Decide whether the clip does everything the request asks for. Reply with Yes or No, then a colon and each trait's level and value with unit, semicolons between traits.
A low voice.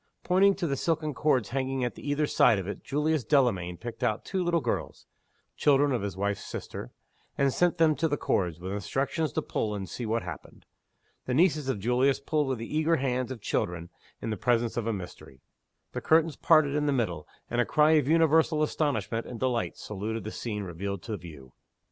Yes: low, 130 Hz